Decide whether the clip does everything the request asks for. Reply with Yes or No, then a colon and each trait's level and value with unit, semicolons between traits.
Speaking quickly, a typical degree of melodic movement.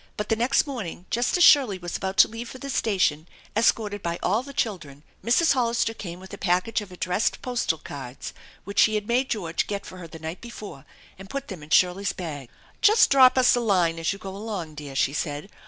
No: fast, 220 wpm; wide, 5.7 semitones